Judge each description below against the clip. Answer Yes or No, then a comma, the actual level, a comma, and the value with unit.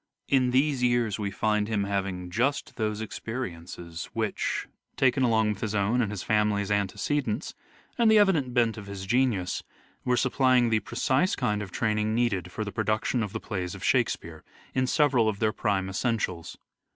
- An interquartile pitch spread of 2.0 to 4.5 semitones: Yes, average, 3.8 semitones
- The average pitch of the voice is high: No, low, 110 Hz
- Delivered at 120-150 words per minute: No, average, 175 wpm